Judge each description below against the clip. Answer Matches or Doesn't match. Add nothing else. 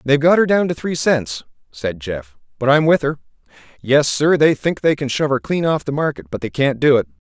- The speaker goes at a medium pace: Doesn't match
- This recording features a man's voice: Matches